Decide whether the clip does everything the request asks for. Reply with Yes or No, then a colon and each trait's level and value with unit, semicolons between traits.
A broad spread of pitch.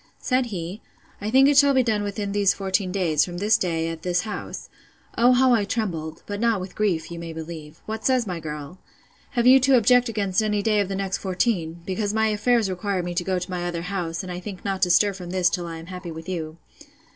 No: average, 3.8 semitones